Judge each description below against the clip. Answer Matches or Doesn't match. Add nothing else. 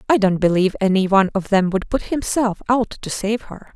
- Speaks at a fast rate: Matches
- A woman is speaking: Matches